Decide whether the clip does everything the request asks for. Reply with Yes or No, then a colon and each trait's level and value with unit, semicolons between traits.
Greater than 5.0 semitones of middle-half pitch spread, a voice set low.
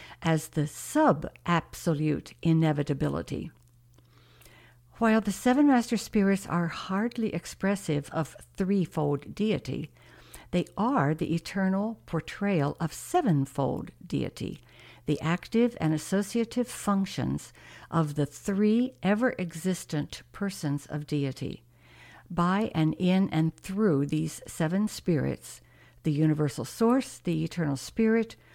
No: wide, 5.4 semitones; medium, 165 Hz